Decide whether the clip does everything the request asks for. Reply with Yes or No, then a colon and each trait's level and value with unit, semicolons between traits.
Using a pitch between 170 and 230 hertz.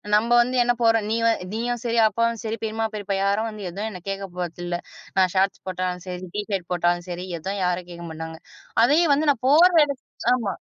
Yes: high, 200 Hz